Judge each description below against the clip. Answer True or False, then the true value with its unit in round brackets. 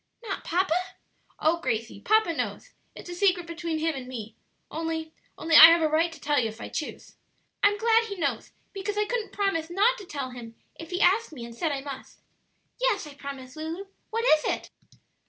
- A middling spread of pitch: False (5.7 semitones)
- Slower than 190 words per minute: False (205 wpm)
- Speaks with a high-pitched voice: True (330 Hz)